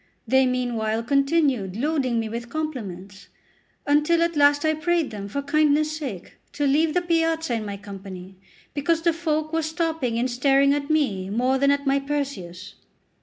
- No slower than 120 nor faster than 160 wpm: No, average, 170 wpm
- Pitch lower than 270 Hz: No, very high, 280 Hz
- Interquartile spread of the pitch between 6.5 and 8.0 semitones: No, average, 5.3 semitones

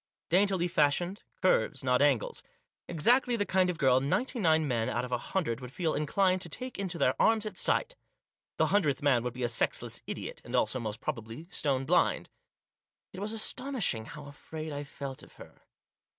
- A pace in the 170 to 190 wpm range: Yes, average, 185 wpm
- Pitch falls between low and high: Yes, medium, 155 Hz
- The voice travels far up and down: Yes, wide, 6.5 semitones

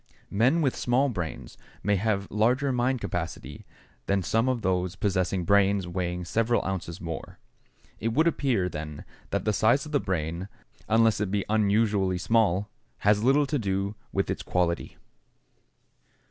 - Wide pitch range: No, average, 3.9 semitones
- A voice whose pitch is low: Yes, low, 100 Hz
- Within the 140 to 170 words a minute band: Yes, average, 150 wpm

